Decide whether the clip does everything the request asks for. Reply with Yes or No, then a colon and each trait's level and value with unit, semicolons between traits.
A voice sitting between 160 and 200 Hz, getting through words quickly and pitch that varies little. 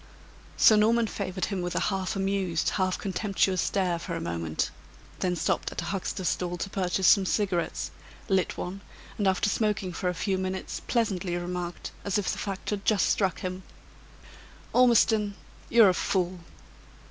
No: high, 190 Hz; average, 165 wpm; narrow, 2.1 semitones